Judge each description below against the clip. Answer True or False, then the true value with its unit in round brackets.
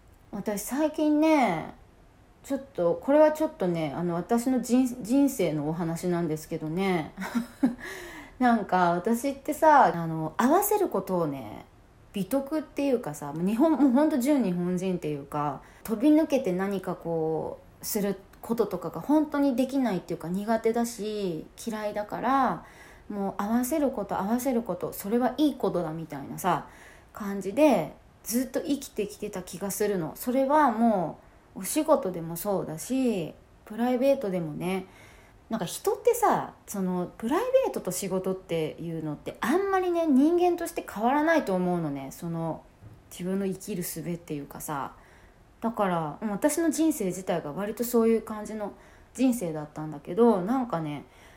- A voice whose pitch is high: True (210 Hz)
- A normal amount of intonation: False (7.6 semitones)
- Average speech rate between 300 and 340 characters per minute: True (320 characters per minute)